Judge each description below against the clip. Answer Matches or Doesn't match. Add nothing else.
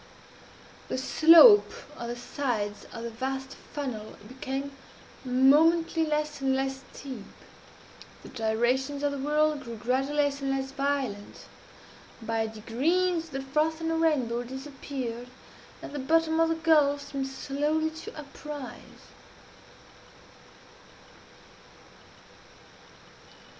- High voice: Matches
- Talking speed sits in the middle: Doesn't match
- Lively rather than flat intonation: Doesn't match